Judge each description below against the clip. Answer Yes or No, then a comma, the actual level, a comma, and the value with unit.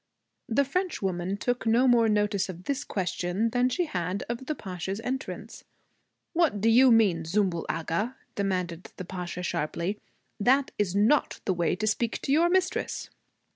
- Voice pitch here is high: Yes, high, 210 Hz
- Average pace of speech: Yes, average, 160 wpm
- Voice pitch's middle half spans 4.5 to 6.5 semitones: Yes, wide, 5.6 semitones